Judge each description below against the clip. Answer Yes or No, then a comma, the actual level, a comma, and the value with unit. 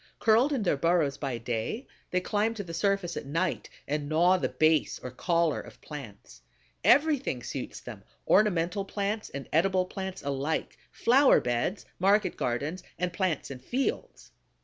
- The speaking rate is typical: Yes, average, 155 wpm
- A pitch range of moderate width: No, wide, 6.0 semitones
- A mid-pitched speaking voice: Yes, medium, 175 Hz